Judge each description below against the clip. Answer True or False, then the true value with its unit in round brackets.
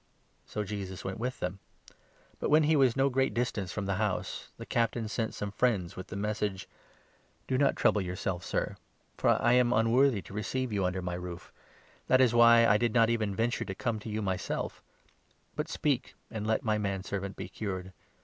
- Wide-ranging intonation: False (3.8 semitones)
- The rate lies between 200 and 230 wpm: True (205 wpm)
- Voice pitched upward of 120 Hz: False (110 Hz)